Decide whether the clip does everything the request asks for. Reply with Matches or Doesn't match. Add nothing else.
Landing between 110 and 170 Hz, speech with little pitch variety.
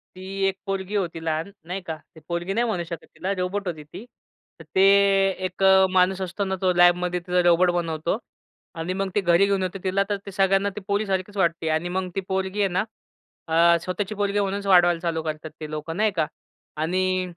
Doesn't match